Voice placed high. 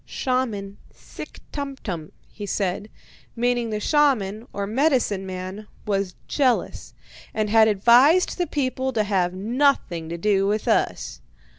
Yes: high, 215 Hz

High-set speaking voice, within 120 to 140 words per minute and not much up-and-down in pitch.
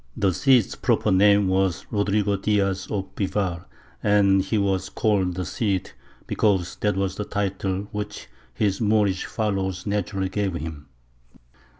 No: low, 100 Hz; slow, 135 wpm; narrow, 1.6 semitones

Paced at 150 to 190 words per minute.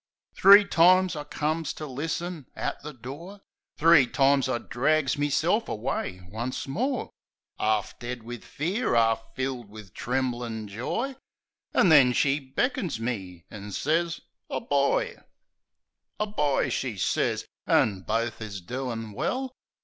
No: slow, 135 wpm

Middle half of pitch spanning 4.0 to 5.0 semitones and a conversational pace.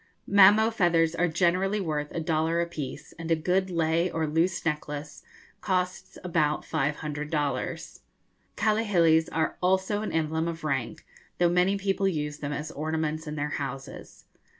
No: average, 3.2 semitones; average, 155 wpm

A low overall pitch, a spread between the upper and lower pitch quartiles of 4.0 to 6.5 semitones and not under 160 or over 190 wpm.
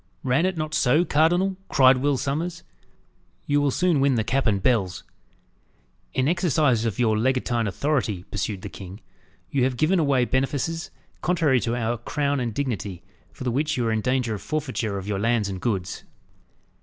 Yes: low, 130 Hz; average, 5.0 semitones; average, 180 wpm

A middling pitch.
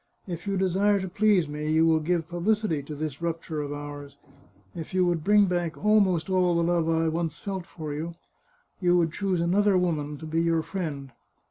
Yes: medium, 170 Hz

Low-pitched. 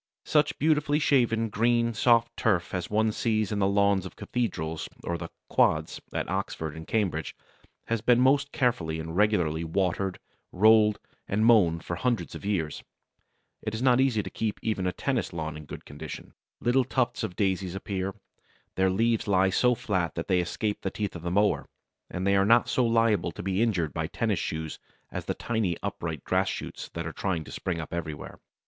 Yes: low, 100 Hz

